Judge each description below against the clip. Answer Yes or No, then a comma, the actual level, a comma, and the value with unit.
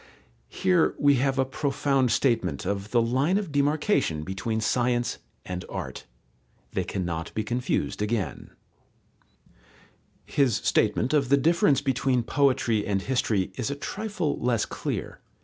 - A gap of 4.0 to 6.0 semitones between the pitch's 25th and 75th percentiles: Yes, average, 4.6 semitones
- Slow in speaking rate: Yes, slow, 130 wpm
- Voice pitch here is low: Yes, low, 125 Hz